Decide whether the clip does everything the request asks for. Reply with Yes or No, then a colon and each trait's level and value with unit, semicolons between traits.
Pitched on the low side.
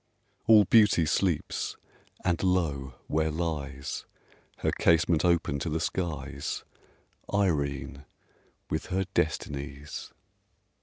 Yes: very low, 80 Hz